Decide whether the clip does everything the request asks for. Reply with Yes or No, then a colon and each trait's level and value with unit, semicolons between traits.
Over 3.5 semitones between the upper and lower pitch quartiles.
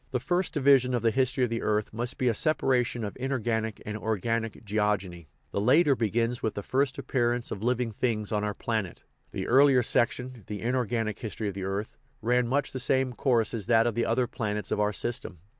No: average, 2.9 semitones